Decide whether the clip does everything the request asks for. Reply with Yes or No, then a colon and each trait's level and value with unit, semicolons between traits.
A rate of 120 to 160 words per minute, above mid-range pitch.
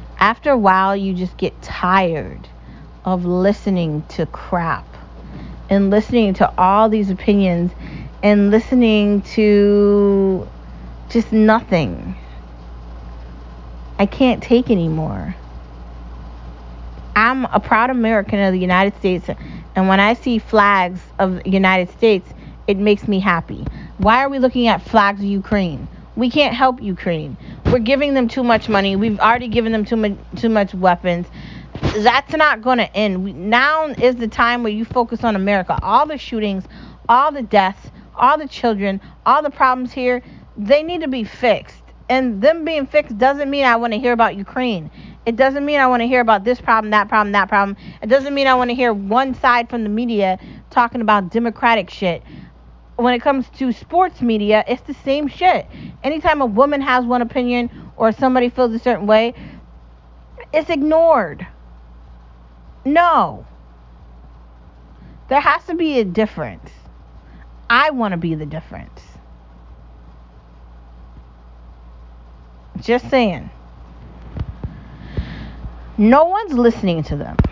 Yes: average, 150 wpm; high, 205 Hz